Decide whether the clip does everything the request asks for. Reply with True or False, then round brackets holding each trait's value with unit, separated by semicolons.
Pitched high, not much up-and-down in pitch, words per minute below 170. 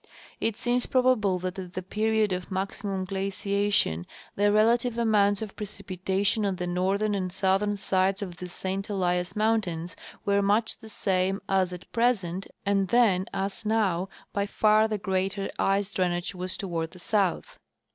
True (195 Hz; 2.3 semitones; 155 wpm)